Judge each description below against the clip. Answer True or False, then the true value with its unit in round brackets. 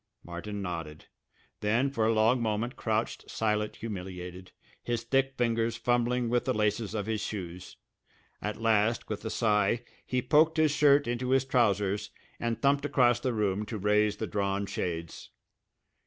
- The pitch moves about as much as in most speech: True (3.0 semitones)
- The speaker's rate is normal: True (155 wpm)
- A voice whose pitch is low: True (110 Hz)